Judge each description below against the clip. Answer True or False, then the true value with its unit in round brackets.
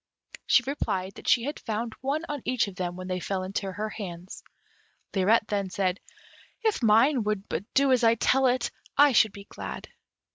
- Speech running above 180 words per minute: True (190 wpm)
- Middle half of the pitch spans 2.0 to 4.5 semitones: False (5.1 semitones)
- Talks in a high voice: True (215 Hz)